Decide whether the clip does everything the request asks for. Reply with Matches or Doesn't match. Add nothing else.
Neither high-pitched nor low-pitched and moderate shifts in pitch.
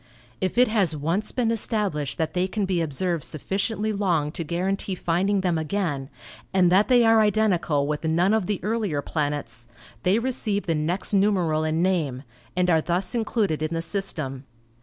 Matches